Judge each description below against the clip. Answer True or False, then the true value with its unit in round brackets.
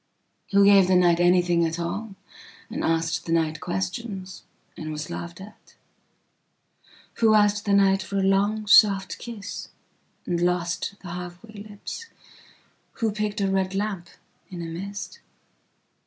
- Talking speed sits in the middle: False (125 wpm)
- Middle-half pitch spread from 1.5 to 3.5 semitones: True (2.8 semitones)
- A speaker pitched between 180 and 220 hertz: True (190 Hz)